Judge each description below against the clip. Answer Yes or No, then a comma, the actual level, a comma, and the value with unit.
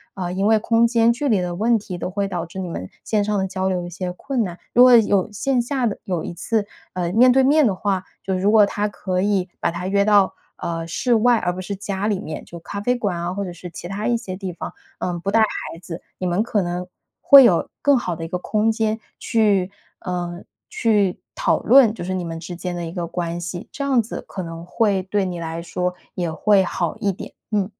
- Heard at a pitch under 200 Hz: Yes, high, 190 Hz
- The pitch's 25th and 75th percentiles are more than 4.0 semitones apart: No, average, 3.7 semitones